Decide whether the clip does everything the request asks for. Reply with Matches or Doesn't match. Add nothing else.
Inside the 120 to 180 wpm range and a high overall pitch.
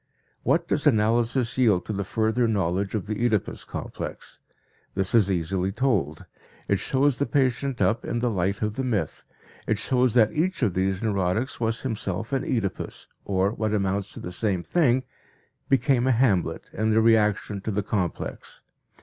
Doesn't match